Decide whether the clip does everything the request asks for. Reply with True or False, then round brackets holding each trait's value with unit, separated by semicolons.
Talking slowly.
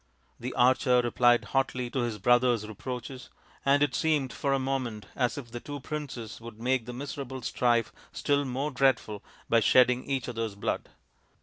False (170 wpm)